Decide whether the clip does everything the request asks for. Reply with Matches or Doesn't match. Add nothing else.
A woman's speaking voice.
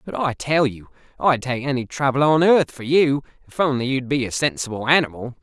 Doesn't match